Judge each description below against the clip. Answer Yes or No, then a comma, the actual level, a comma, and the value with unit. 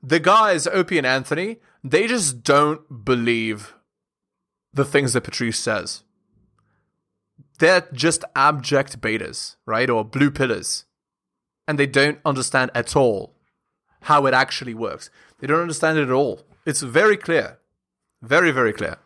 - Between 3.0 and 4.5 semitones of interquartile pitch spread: Yes, average, 3.5 semitones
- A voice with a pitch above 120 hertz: Yes, medium, 140 Hz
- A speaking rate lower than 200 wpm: Yes, average, 140 wpm